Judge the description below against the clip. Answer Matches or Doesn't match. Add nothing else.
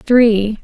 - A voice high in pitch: Matches